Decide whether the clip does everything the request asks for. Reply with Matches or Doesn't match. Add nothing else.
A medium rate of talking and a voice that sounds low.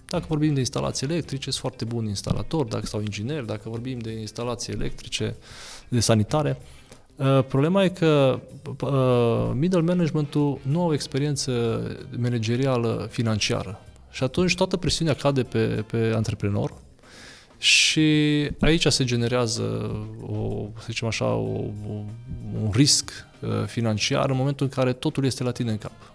Matches